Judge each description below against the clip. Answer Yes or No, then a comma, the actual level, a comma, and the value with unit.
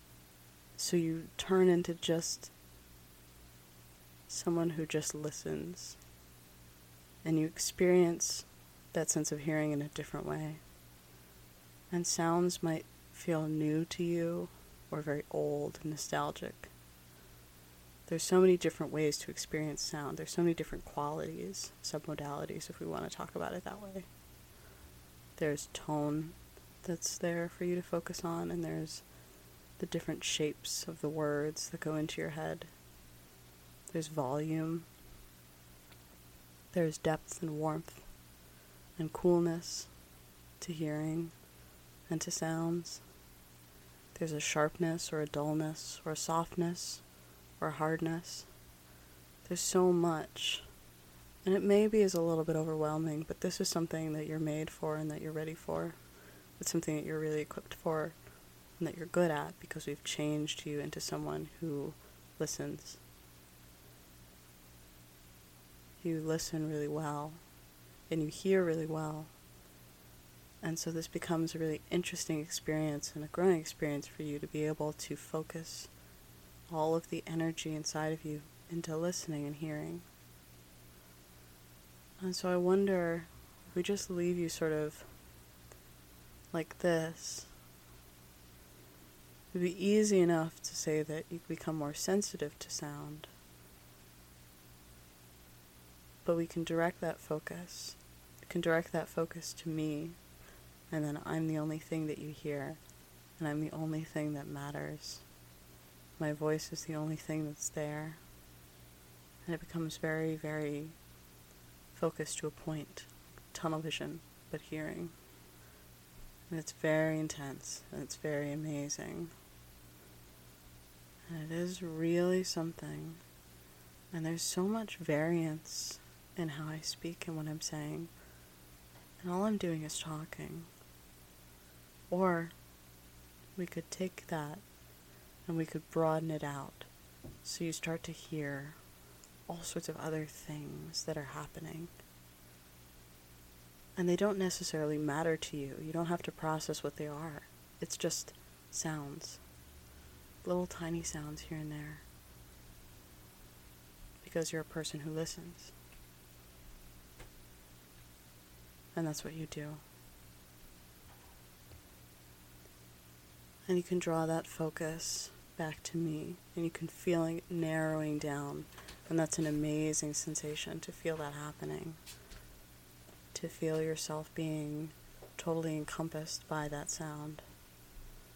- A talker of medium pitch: Yes, medium, 150 Hz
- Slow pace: Yes, slow, 130 wpm